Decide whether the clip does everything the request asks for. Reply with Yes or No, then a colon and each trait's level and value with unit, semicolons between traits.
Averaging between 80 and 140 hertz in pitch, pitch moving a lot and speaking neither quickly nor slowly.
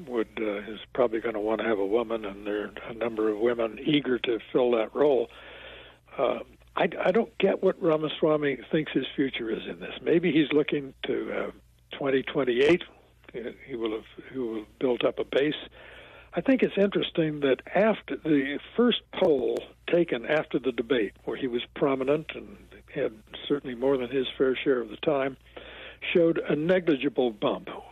Yes: low, 135 Hz; wide, 5.9 semitones; average, 180 wpm